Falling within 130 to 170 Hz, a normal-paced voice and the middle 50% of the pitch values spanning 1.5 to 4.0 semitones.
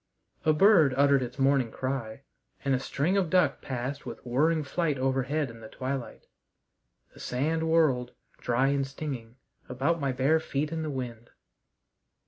Yes: low, 135 Hz; average, 155 wpm; average, 3.5 semitones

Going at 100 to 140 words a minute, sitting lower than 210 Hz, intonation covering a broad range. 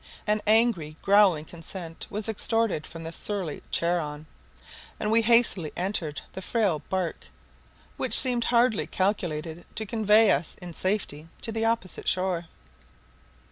No: slow, 135 wpm; high, 190 Hz; average, 4.9 semitones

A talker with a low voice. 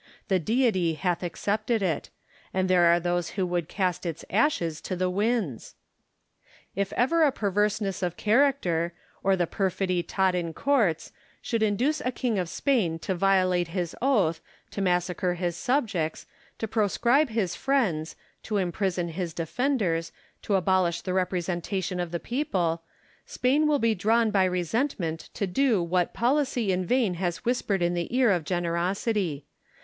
No: high, 190 Hz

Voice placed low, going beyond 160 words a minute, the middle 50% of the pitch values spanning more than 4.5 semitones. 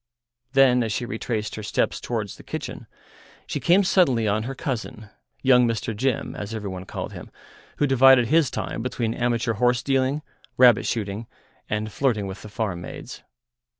No: low, 115 Hz; average, 170 wpm; average, 3.5 semitones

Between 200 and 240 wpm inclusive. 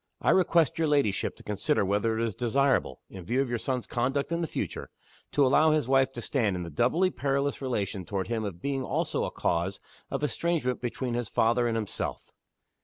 Yes: fast, 205 wpm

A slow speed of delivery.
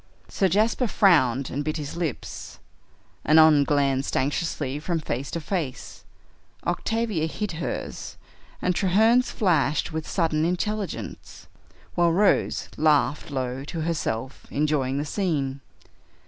Yes: slow, 120 wpm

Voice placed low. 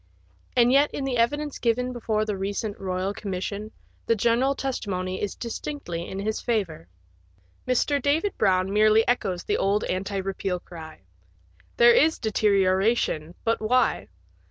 No: high, 215 Hz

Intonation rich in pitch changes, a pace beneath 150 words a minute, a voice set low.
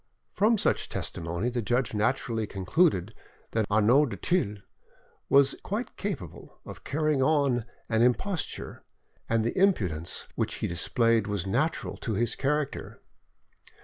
Yes: wide, 6.3 semitones; slow, 135 wpm; low, 120 Hz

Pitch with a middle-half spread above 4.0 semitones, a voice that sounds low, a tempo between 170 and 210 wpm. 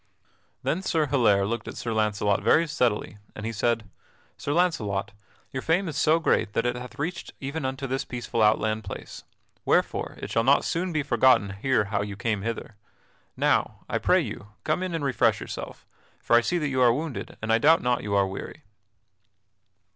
Yes: wide, 5.6 semitones; low, 125 Hz; average, 190 wpm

